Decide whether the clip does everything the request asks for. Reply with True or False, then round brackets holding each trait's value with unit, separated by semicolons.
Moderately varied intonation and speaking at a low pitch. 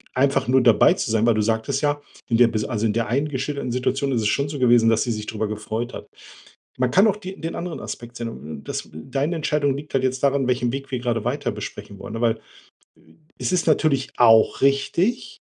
True (3.8 semitones; 125 Hz)